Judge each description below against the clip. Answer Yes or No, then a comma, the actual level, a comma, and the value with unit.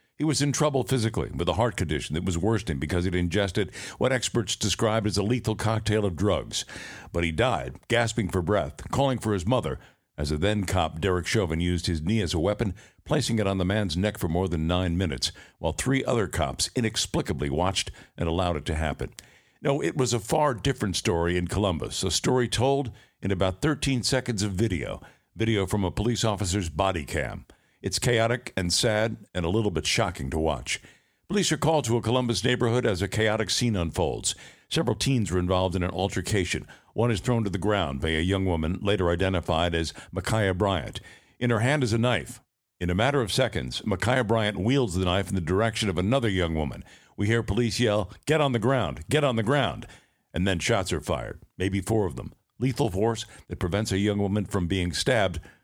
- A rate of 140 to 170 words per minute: No, fast, 205 wpm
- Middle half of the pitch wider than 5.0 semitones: No, average, 4.5 semitones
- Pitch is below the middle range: Yes, low, 105 Hz